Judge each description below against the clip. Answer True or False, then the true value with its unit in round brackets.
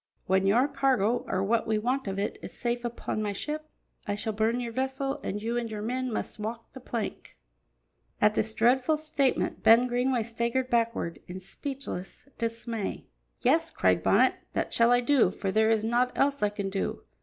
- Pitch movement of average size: True (3.2 semitones)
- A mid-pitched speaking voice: False (230 Hz)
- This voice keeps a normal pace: True (190 wpm)